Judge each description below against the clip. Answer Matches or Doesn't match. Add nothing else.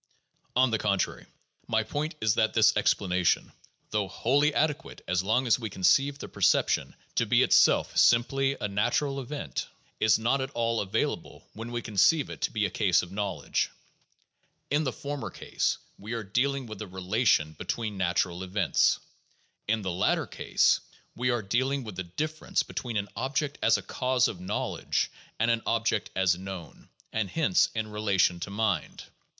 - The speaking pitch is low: Matches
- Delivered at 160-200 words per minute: Matches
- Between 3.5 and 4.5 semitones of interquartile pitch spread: Doesn't match